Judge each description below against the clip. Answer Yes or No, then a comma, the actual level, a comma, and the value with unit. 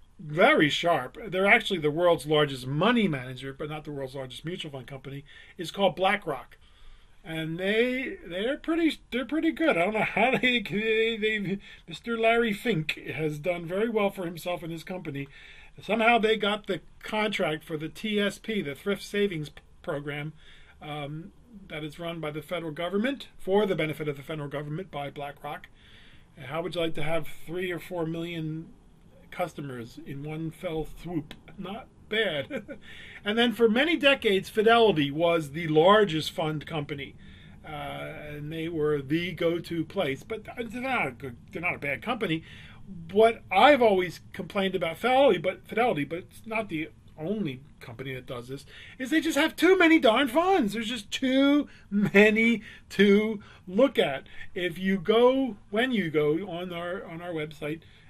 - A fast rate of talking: No, average, 170 wpm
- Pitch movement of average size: No, wide, 6.1 semitones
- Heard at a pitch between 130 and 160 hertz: No, medium, 175 Hz